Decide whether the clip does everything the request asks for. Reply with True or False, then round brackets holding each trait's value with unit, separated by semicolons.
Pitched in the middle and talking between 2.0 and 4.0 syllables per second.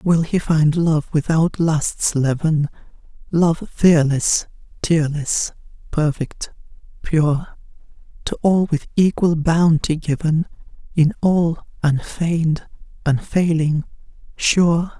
True (160 Hz; 3.3 syllables/s)